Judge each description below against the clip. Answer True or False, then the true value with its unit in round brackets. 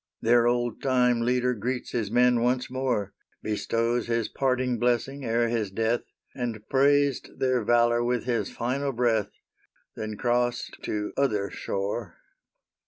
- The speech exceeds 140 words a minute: False (135 wpm)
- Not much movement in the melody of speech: True (1.6 semitones)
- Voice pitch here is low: True (120 Hz)